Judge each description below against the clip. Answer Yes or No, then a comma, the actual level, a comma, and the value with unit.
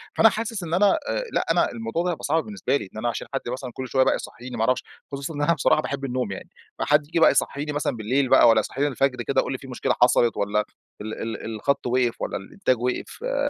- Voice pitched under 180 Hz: Yes, low, 135 Hz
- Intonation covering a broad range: No, average, 4.1 semitones